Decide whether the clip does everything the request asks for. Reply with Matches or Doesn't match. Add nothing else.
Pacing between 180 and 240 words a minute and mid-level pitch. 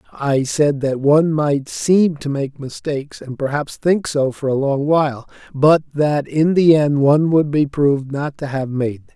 Matches